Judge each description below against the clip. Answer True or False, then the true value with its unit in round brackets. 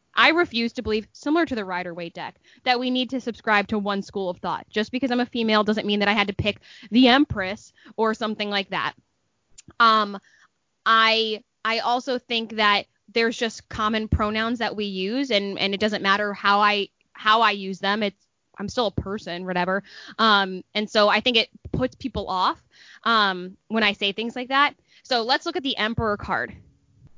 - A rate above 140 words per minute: True (200 wpm)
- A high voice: True (215 Hz)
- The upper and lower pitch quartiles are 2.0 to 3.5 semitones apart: True (2.6 semitones)